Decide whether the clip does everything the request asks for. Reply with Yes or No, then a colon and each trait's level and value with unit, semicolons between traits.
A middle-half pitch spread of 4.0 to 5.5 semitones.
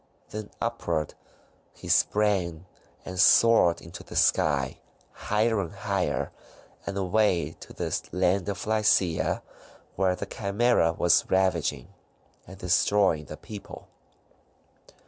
No: average, 3.5 semitones